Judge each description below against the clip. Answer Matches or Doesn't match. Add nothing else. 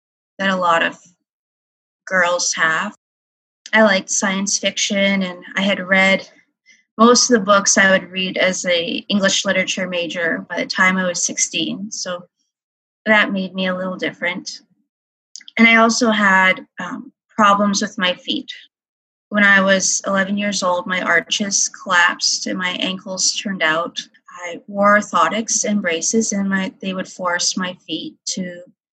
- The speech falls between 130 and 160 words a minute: Matches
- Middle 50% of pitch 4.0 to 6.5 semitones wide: Doesn't match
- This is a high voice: Matches